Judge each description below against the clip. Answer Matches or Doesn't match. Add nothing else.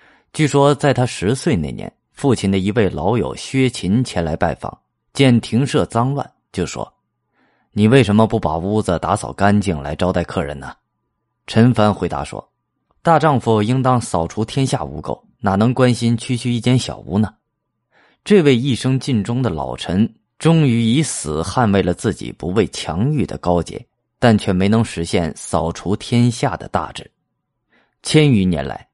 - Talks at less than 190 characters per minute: Doesn't match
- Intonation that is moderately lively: Doesn't match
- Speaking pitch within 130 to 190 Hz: Doesn't match